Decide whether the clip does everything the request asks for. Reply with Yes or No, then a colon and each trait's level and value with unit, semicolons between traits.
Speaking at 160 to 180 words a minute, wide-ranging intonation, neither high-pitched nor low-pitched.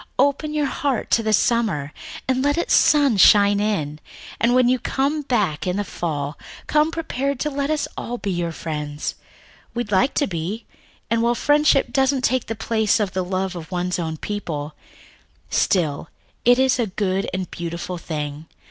No: average, 175 wpm; wide, 7.1 semitones; high, 210 Hz